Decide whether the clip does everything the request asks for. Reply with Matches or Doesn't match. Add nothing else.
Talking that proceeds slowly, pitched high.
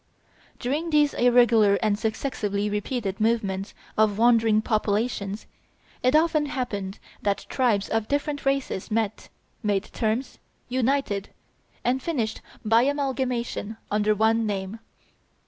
Matches